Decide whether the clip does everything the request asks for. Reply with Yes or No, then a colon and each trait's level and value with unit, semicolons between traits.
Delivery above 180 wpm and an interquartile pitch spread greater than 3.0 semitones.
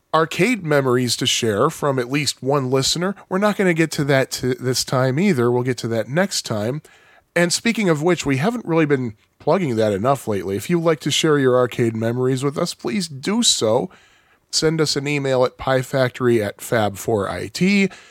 Yes: average, 200 wpm; wide, 5.5 semitones